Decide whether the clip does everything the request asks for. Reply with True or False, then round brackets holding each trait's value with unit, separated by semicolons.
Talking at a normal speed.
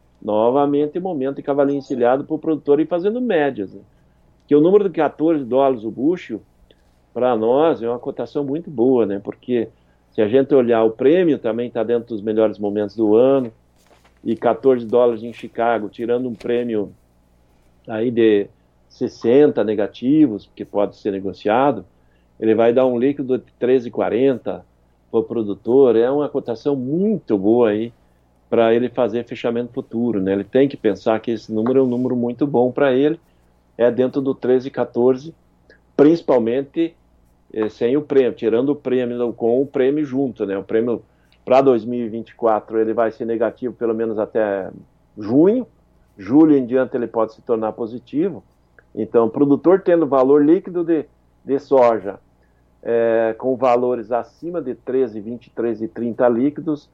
True (160 wpm)